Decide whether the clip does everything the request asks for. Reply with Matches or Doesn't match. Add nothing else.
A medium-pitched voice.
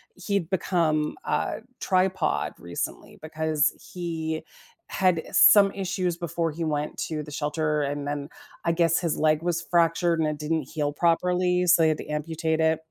Matches